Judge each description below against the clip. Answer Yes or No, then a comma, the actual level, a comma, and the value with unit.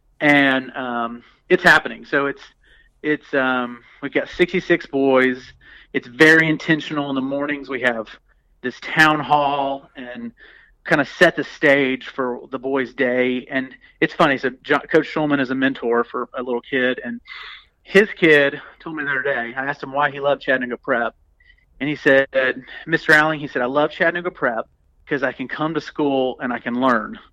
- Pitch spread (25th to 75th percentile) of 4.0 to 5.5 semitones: No, average, 2.9 semitones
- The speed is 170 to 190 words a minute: Yes, average, 185 wpm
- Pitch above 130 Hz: Yes, medium, 140 Hz